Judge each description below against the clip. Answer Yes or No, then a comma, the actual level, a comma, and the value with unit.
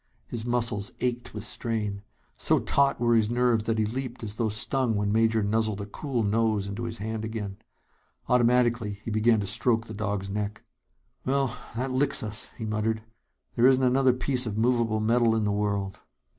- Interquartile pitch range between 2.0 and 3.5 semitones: Yes, narrow, 2.4 semitones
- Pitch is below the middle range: Yes, low, 110 Hz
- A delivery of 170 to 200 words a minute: Yes, average, 185 wpm